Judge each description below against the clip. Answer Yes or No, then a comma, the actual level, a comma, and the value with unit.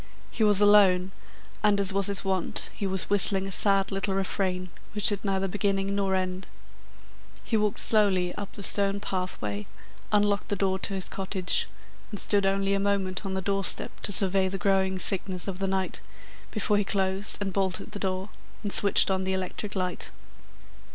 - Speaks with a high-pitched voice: Yes, high, 195 Hz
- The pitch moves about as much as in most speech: No, narrow, 1.2 semitones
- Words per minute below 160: No, average, 180 wpm